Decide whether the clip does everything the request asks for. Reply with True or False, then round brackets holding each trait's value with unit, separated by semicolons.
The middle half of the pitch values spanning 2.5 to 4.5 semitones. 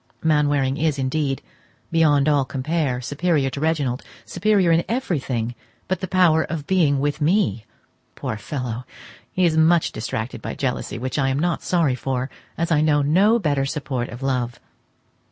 True (3.9 semitones)